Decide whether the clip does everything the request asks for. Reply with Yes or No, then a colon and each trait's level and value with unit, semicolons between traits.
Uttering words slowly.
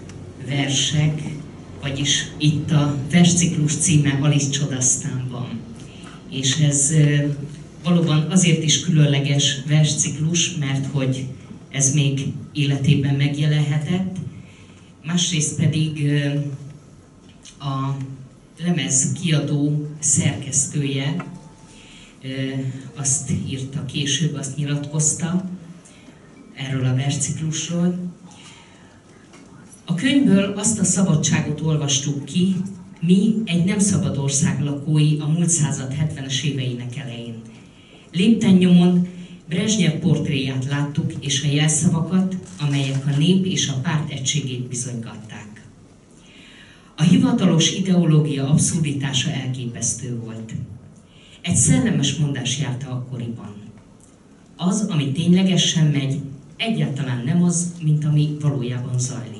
Yes: slow, 95 wpm